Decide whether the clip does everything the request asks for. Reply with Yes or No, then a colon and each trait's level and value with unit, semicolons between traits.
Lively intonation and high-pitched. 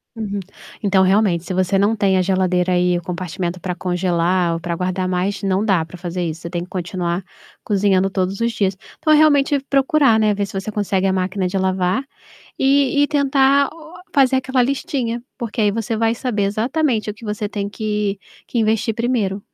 No: average, 4.0 semitones; high, 200 Hz